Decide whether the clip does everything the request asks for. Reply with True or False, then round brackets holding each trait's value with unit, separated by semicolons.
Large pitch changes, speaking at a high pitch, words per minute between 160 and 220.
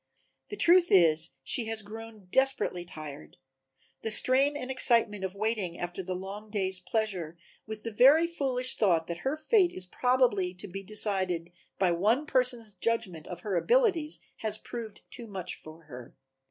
True (5.8 semitones; 210 Hz; 165 wpm)